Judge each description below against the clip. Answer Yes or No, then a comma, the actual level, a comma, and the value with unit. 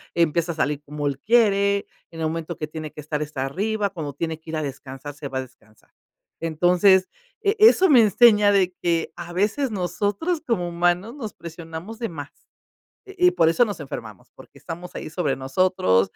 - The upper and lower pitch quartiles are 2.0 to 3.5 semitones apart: No, average, 5.2 semitones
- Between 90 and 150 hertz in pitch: No, medium, 170 Hz